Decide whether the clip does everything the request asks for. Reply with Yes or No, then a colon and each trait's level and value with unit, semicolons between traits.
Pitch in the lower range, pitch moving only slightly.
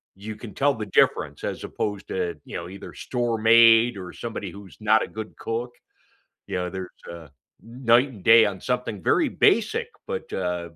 No: low, 110 Hz; average, 3.6 semitones